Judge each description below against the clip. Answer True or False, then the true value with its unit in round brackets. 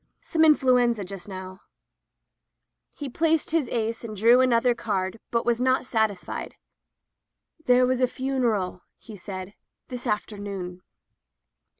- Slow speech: True (120 wpm)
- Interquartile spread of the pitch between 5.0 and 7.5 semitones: False (4.2 semitones)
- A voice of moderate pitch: False (230 Hz)